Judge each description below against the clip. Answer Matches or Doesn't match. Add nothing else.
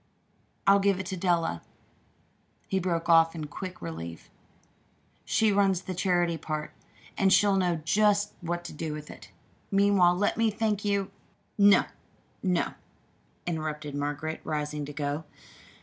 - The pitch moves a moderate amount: Matches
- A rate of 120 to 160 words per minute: Matches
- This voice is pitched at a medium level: Matches